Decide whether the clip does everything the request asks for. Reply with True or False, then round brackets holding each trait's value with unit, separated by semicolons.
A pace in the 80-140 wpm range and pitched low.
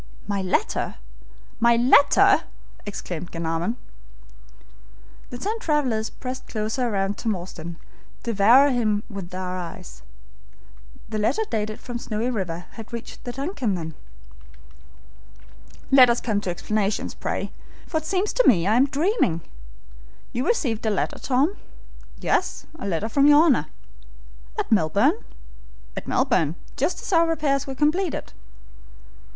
False (135 wpm; 230 Hz)